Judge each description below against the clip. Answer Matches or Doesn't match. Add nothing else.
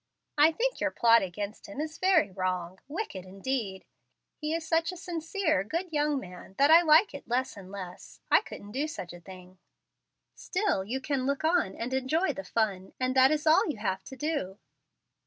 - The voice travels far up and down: Matches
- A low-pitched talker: Doesn't match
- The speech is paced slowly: Doesn't match